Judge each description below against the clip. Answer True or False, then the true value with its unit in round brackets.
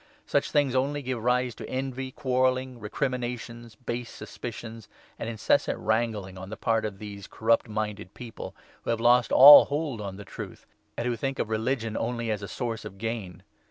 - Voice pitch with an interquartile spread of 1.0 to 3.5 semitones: True (2.8 semitones)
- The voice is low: True (115 Hz)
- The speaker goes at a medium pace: True (185 wpm)